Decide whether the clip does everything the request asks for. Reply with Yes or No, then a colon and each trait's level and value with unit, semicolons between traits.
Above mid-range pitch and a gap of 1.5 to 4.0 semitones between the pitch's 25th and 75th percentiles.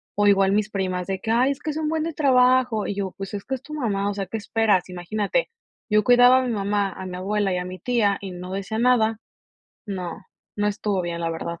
No: high, 205 Hz; average, 4.4 semitones